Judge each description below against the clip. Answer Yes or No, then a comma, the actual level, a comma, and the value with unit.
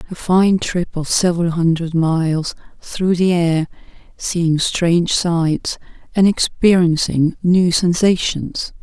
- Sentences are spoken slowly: Yes, slow, 115 wpm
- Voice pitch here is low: No, medium, 170 Hz